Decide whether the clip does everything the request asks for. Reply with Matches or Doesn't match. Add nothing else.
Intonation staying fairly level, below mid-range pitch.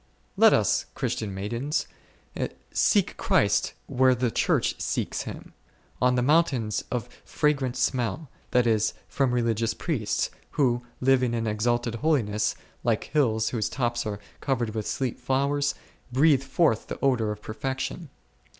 Doesn't match